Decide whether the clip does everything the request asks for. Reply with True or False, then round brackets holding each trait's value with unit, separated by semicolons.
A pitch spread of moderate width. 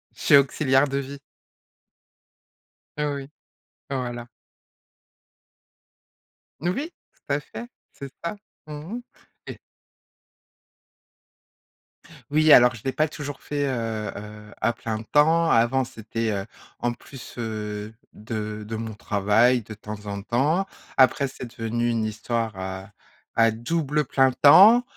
True (4.7 semitones)